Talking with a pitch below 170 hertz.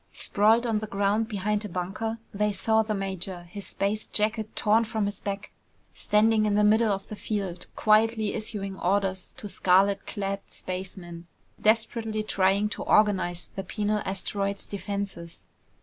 No: high, 205 Hz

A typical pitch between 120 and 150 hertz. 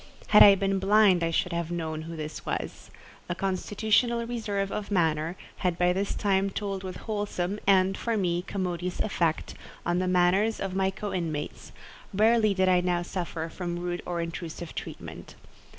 No: medium, 185 Hz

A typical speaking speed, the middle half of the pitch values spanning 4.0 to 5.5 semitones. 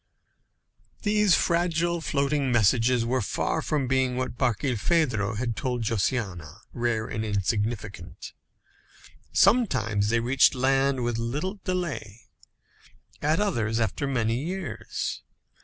No: slow, 110 wpm; average, 5.0 semitones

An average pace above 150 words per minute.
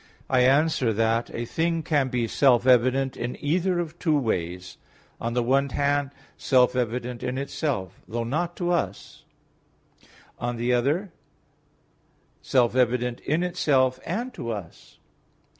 No: average, 140 wpm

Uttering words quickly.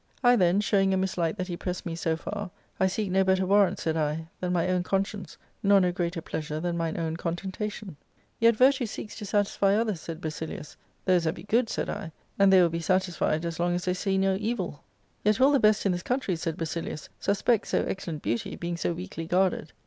Yes: fast, 240 wpm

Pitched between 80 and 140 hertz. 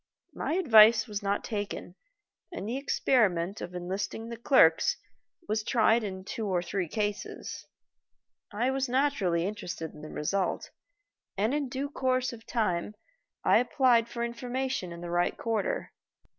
No: high, 220 Hz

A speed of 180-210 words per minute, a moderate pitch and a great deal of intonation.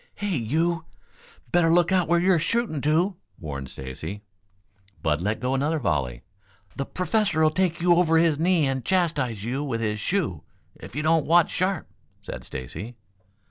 No: average, 160 wpm; medium, 155 Hz; wide, 7.2 semitones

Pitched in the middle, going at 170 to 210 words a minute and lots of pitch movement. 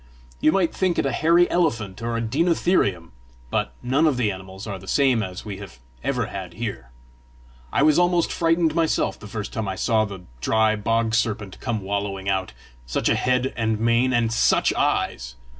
No: low, 115 Hz; average, 190 wpm; wide, 5.8 semitones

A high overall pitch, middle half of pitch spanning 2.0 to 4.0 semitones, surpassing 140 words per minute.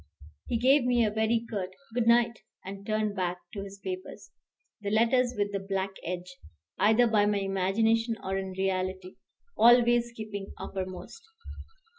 Yes: high, 210 Hz; average, 3.3 semitones; average, 150 wpm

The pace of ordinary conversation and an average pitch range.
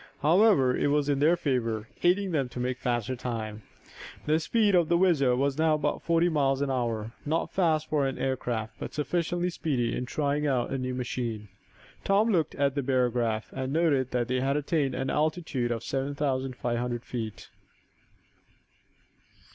Yes: average, 180 wpm; average, 4.0 semitones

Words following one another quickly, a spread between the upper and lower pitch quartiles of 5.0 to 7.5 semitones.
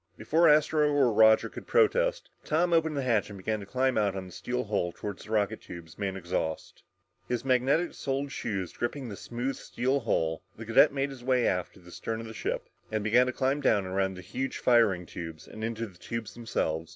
Yes: fast, 215 wpm; wide, 5.6 semitones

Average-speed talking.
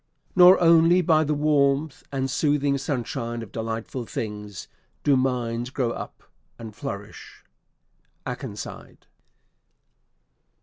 No: slow, 100 wpm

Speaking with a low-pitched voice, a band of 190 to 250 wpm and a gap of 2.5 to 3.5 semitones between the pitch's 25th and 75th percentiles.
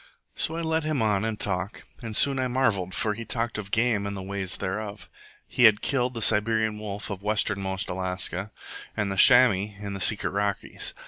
Yes: low, 105 Hz; average, 195 wpm; average, 2.8 semitones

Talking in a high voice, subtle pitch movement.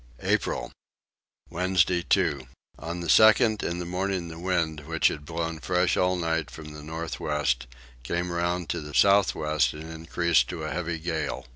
No: very low, 85 Hz; narrow, 2.2 semitones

